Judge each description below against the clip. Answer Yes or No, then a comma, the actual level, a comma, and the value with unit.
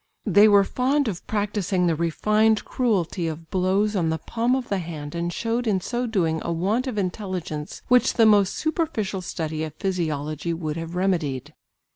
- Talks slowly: No, average, 175 wpm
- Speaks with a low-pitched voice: No, high, 190 Hz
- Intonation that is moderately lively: Yes, average, 4.7 semitones